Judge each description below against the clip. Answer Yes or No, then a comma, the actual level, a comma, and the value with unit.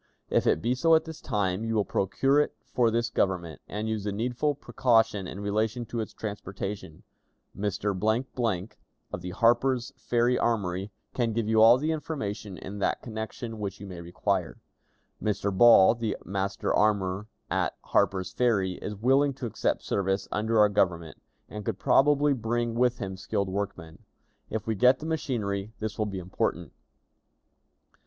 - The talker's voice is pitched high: No, low, 110 Hz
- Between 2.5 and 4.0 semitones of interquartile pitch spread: Yes, average, 3.5 semitones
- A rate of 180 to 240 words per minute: No, average, 160 wpm